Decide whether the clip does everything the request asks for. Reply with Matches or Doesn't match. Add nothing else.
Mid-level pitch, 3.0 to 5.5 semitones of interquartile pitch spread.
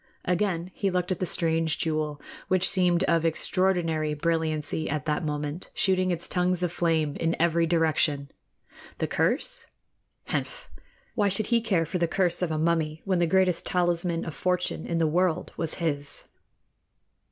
Doesn't match